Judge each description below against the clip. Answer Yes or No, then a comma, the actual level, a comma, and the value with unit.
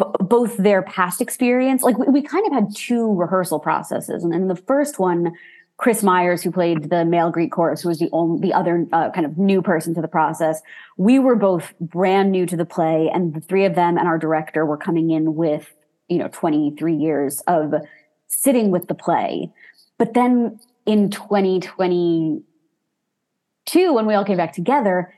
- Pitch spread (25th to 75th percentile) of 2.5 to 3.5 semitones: No, average, 4.1 semitones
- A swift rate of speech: No, average, 195 wpm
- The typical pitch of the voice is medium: Yes, medium, 180 Hz